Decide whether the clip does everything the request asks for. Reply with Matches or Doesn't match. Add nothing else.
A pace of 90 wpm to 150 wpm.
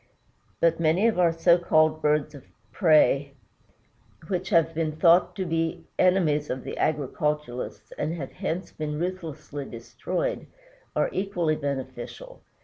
Matches